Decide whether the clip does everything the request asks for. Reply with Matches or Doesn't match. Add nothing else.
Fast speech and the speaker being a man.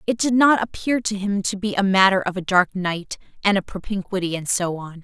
Doesn't match